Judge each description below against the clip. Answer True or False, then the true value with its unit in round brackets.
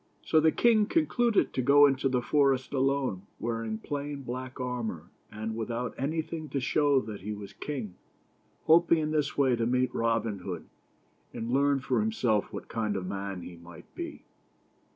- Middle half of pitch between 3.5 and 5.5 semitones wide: True (4.9 semitones)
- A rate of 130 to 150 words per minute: False (175 wpm)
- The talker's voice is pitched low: True (130 Hz)